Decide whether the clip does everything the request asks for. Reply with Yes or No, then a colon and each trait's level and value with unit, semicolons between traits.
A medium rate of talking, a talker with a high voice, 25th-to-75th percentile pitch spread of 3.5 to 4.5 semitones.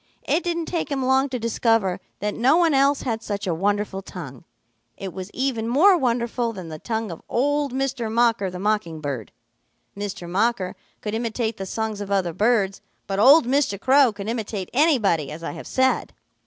No: average, 185 wpm; high, 225 Hz; average, 5.0 semitones